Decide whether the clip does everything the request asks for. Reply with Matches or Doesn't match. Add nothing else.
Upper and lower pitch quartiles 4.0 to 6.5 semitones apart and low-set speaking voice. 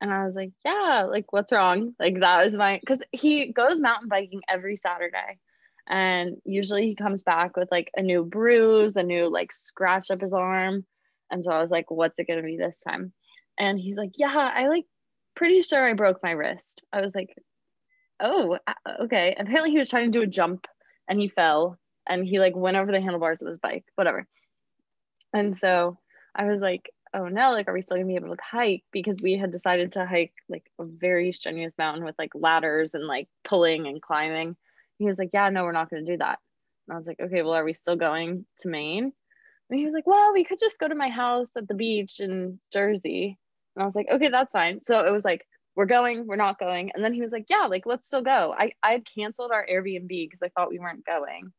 Doesn't match